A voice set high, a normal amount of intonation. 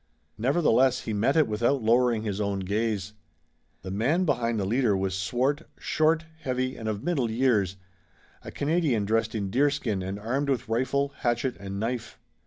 No: low, 115 Hz; average, 4.5 semitones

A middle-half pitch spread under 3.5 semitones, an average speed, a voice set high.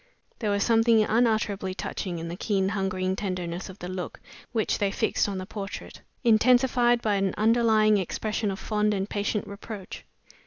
Yes: narrow, 2.5 semitones; average, 165 wpm; high, 205 Hz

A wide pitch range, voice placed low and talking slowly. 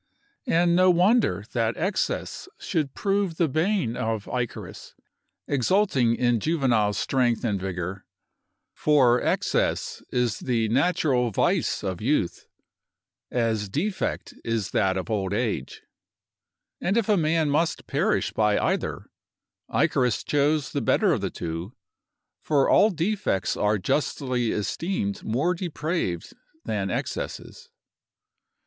Yes: wide, 7.6 semitones; low, 125 Hz; slow, 120 wpm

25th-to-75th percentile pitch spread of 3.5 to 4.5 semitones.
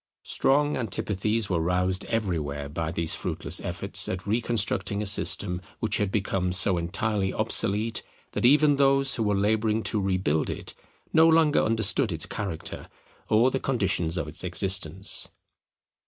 Yes: average, 3.9 semitones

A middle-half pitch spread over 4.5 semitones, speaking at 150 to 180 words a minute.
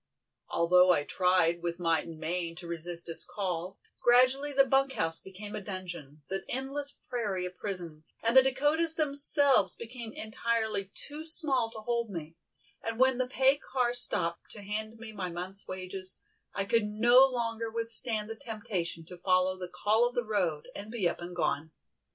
Yes: wide, 5.4 semitones; average, 175 wpm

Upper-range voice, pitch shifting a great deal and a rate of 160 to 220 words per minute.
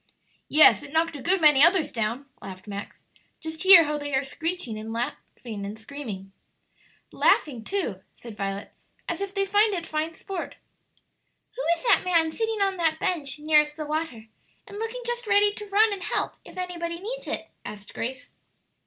Yes: very high, 320 Hz; wide, 7.4 semitones; average, 175 wpm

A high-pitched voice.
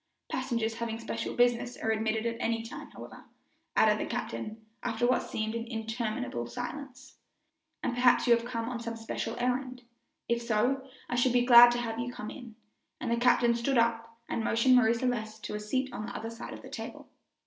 Yes: high, 235 Hz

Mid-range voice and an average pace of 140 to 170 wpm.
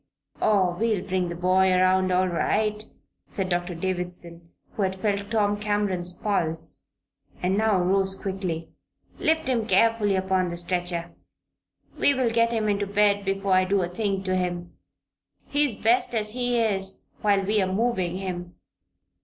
No: high, 195 Hz; average, 155 wpm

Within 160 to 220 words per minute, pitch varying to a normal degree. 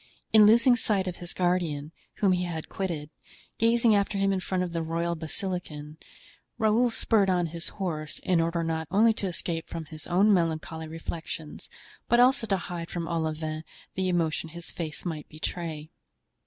Yes: average, 170 wpm; average, 3.4 semitones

